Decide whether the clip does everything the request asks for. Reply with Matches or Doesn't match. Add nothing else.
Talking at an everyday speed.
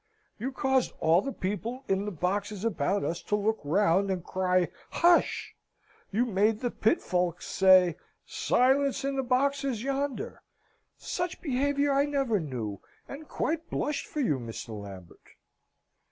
Matches